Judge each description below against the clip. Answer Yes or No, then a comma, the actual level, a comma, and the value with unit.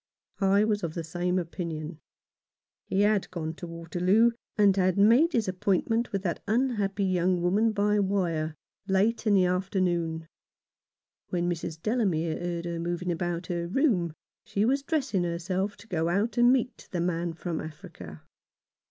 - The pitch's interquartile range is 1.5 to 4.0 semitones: Yes, average, 3.5 semitones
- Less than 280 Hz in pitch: Yes, medium, 185 Hz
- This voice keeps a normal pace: Yes, average, 165 wpm